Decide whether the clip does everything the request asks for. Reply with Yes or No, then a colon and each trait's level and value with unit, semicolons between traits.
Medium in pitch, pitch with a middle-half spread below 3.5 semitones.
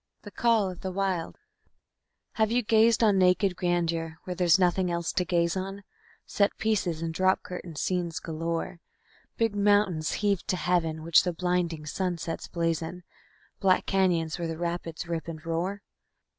Yes: medium, 180 Hz; narrow, 2.6 semitones